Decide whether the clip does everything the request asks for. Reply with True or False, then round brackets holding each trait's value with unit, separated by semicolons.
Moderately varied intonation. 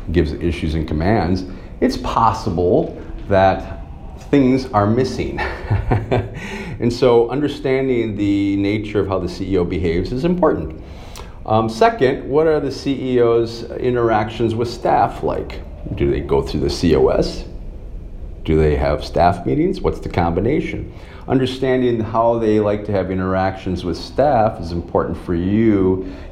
False (5.7 semitones)